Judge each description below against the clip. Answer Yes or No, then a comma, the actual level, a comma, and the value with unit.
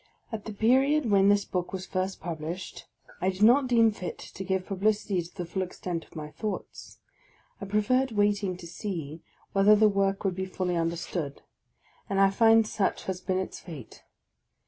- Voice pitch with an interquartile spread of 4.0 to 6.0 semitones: No, average, 2.8 semitones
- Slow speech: No, average, 180 wpm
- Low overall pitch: No, high, 195 Hz